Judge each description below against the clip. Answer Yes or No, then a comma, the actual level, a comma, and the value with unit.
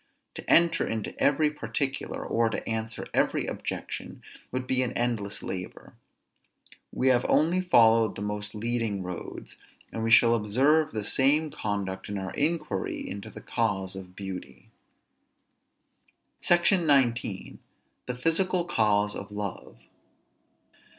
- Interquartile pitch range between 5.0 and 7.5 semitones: Yes, average, 5.3 semitones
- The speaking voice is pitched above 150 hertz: No, low, 115 Hz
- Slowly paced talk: Yes, slow, 130 wpm